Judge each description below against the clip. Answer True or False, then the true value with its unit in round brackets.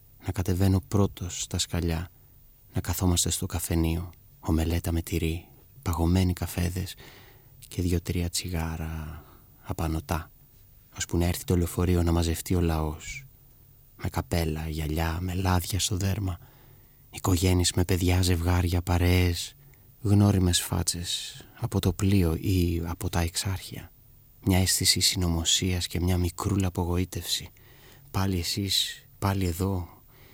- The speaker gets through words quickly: False (115 wpm)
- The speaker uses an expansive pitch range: False (2.5 semitones)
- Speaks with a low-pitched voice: True (90 Hz)